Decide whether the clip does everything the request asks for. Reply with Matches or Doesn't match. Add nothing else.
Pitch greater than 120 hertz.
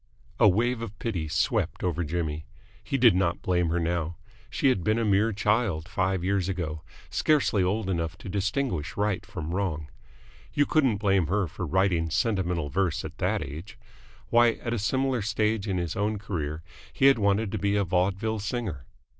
Doesn't match